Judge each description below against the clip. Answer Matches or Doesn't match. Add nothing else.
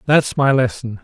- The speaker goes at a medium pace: Matches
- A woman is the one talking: Doesn't match